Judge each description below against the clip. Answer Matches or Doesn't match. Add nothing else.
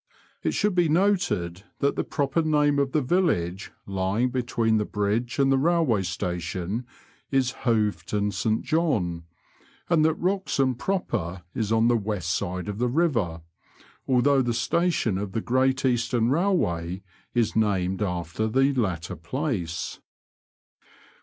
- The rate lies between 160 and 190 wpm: Doesn't match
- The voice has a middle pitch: Doesn't match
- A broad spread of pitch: Matches